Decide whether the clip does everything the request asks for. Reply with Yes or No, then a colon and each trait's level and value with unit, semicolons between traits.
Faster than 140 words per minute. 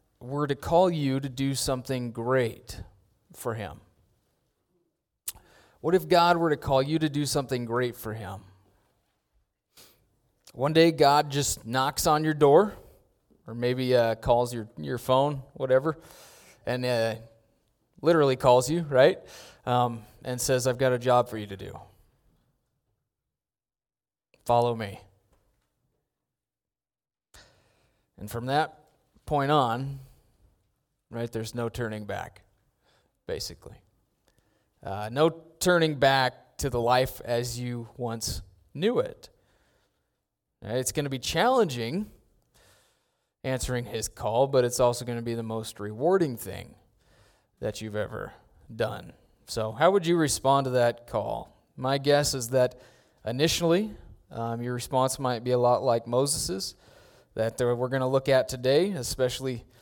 No: slow, 135 wpm